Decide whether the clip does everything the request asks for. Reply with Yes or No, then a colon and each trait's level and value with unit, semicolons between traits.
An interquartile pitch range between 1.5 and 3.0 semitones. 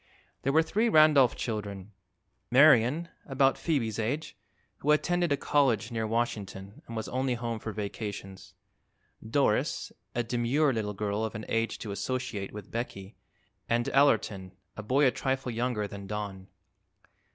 No: average, 4.3 semitones